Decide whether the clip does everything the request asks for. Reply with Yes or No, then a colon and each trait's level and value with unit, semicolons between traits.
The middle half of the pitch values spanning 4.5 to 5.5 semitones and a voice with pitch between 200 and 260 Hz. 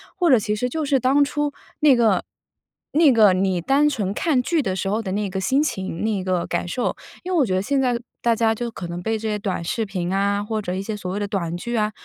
Yes: average, 5.2 semitones; high, 215 Hz